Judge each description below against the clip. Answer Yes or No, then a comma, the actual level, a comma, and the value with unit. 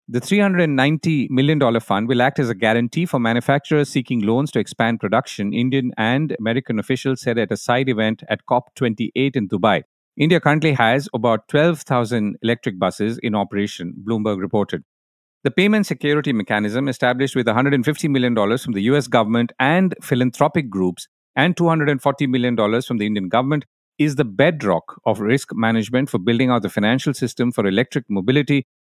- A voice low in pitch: Yes, low, 125 Hz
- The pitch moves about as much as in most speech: Yes, average, 4.2 semitones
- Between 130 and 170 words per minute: Yes, average, 160 wpm